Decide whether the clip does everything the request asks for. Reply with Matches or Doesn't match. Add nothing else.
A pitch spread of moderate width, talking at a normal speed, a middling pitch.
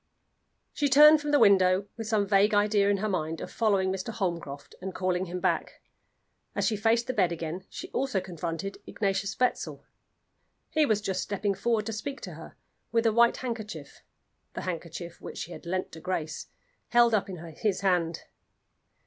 Doesn't match